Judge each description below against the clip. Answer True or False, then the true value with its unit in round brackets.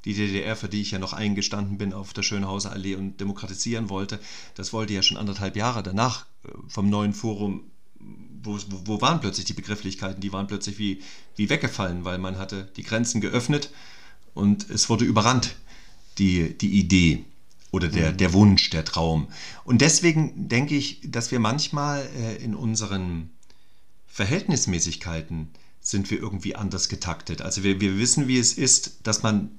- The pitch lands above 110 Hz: False (100 Hz)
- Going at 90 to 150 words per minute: False (165 wpm)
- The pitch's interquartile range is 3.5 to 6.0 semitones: False (3.1 semitones)